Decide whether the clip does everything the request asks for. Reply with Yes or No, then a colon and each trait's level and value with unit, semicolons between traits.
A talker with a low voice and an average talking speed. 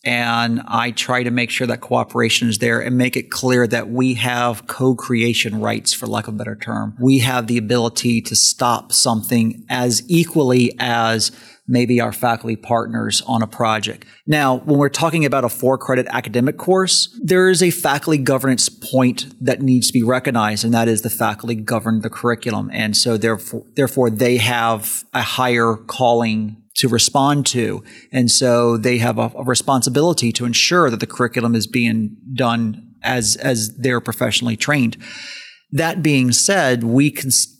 Yes: low, 120 Hz; average, 175 wpm